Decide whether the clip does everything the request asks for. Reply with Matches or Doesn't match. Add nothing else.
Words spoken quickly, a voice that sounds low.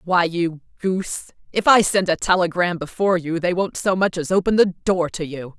Doesn't match